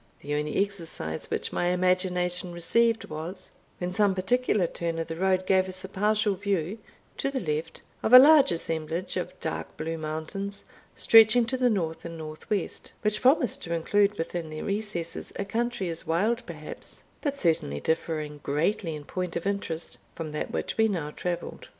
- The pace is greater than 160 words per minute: Yes, average, 175 wpm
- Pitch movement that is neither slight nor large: Yes, average, 4.1 semitones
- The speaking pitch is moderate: Yes, medium, 180 Hz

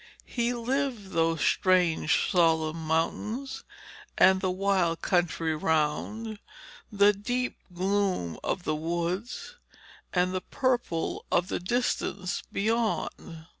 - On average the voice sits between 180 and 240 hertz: Yes, medium, 185 Hz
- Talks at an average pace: No, slow, 105 wpm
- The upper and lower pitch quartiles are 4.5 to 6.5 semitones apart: Yes, average, 5.1 semitones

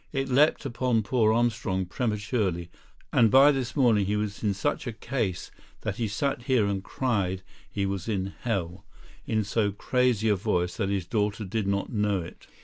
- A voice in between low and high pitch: No, low, 105 Hz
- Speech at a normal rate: Yes, average, 180 wpm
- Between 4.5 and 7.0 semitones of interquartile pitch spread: No, average, 3.7 semitones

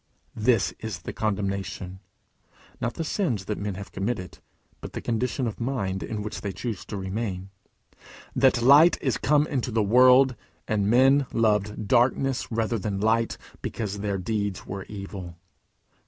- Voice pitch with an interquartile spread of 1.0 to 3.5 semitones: No, average, 3.9 semitones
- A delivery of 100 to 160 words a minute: Yes, average, 155 wpm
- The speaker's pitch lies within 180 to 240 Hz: No, low, 110 Hz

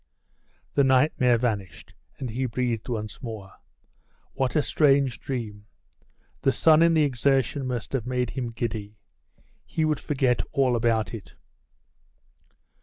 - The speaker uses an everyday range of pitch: Yes, average, 3.3 semitones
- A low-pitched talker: Yes, low, 125 Hz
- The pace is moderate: No, slow, 130 wpm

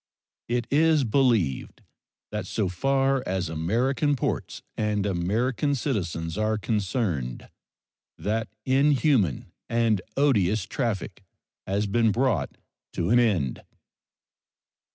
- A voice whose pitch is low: Yes, low, 110 Hz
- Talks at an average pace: No, slow, 100 wpm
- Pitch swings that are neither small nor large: No, wide, 5.7 semitones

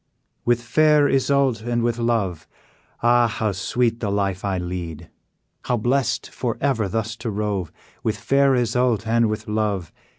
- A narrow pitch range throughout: No, average, 3.3 semitones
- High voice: No, low, 115 Hz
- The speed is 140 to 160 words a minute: Yes, average, 155 wpm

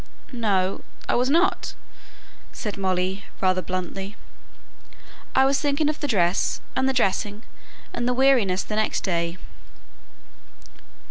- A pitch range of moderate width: No, wide, 6.1 semitones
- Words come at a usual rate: No, slow, 125 wpm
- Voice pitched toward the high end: Yes, high, 210 Hz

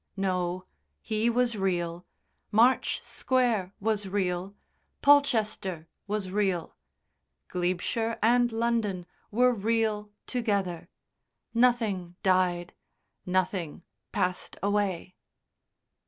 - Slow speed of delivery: Yes, slow, 80 wpm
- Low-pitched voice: No, high, 200 Hz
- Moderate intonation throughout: Yes, average, 3.9 semitones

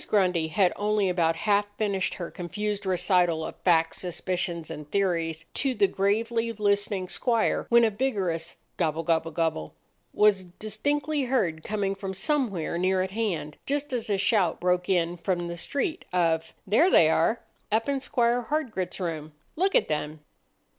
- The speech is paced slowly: No, average, 155 wpm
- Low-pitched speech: No, high, 190 Hz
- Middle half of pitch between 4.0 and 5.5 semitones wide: Yes, average, 4.5 semitones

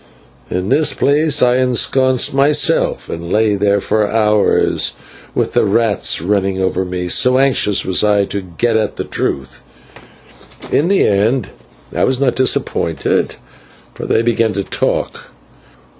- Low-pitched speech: Yes, low, 105 Hz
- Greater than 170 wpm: No, average, 145 wpm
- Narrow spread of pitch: No, average, 4.8 semitones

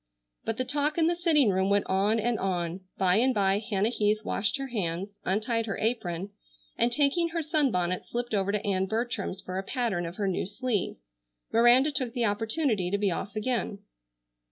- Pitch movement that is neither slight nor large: Yes, average, 4.4 semitones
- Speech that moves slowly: No, average, 190 wpm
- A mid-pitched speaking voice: No, high, 215 Hz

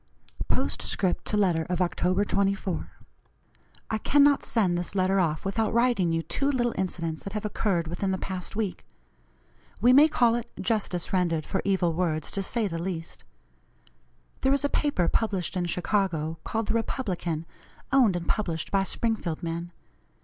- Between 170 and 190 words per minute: No, average, 160 wpm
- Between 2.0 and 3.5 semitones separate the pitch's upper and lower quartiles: No, average, 4.3 semitones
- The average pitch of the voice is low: No, high, 190 Hz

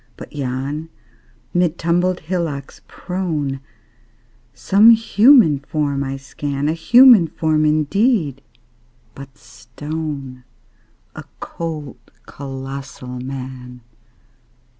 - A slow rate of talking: Yes, slow, 85 wpm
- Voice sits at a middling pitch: Yes, medium, 150 Hz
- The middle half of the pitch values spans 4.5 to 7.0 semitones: No, average, 4.0 semitones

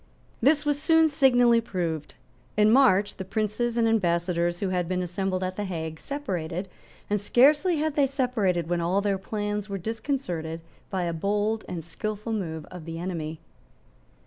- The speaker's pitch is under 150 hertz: No, high, 200 Hz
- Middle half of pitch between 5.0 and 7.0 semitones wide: Yes, average, 5.3 semitones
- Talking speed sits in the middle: Yes, average, 165 wpm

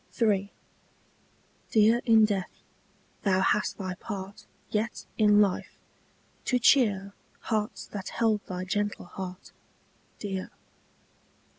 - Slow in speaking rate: Yes, slow, 105 wpm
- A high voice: Yes, high, 205 Hz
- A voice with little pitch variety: Yes, narrow, 2.3 semitones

